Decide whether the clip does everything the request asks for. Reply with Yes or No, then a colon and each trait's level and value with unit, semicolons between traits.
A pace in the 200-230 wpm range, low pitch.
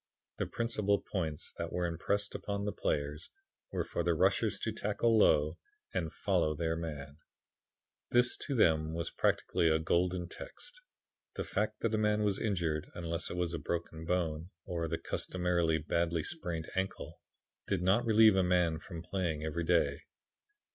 No: average, 160 wpm; very low, 85 Hz